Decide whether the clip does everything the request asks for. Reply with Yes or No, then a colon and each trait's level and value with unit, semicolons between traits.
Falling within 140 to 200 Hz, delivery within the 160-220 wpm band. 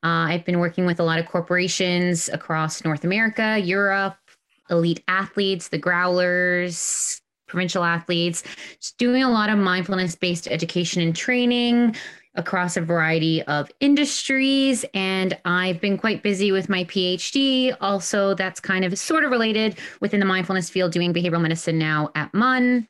No: medium, 185 Hz; average, 150 wpm